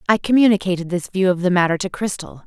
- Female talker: Yes, female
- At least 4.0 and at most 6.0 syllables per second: No, 6.6 syllables/s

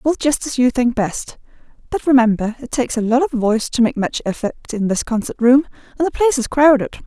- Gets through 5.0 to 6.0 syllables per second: Yes, 5.8 syllables/s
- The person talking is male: No, female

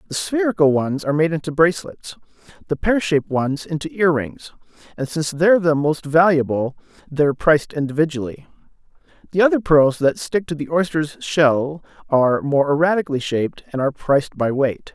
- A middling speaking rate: Yes, average, 160 wpm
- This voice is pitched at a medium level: Yes, medium, 155 Hz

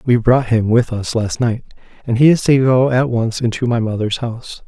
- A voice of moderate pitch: No, low, 120 Hz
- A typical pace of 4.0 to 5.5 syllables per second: Yes, 5.1 syllables/s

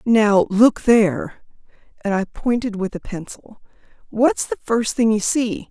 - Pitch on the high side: Yes, high, 220 Hz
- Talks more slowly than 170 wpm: Yes, average, 160 wpm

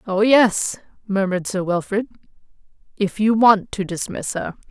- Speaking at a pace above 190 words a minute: No, average, 140 wpm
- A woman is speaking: Yes, female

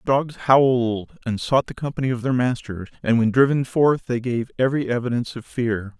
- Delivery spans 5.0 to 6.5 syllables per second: Yes, 5.3 syllables/s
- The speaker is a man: Yes, male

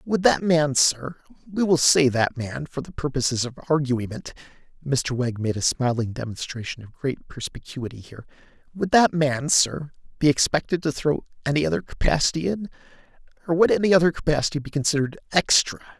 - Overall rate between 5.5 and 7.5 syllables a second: Yes, 5.6 syllables/s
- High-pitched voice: No, medium, 140 Hz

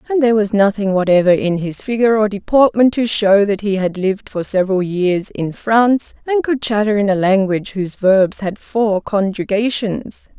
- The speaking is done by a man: No, female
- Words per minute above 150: Yes, average, 185 wpm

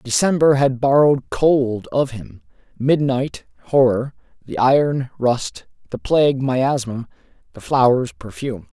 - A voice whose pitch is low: Yes, low, 130 Hz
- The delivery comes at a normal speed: No, slow, 115 wpm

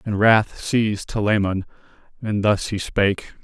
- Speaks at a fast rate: No, average, 140 wpm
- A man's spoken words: Yes, male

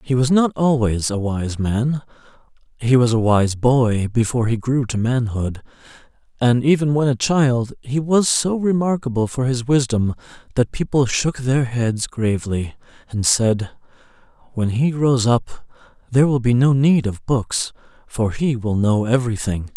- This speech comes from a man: Yes, male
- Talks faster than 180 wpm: No, average, 160 wpm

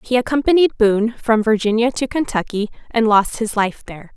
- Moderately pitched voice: No, high, 225 Hz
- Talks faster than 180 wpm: No, average, 175 wpm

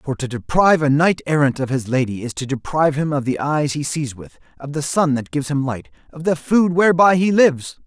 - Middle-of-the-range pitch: Yes, medium, 145 Hz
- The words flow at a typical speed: No, fast, 245 wpm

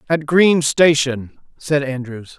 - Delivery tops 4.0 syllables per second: No, 3.5 syllables/s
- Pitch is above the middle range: No, medium, 145 Hz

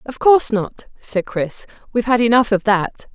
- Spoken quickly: No, average, 190 wpm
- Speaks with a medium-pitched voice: No, high, 225 Hz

